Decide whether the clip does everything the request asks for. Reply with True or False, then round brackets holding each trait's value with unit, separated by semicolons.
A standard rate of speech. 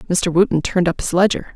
False (230 wpm)